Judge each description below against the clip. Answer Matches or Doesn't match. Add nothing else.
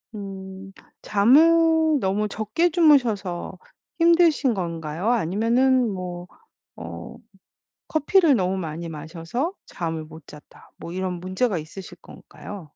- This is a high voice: Matches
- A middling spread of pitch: Doesn't match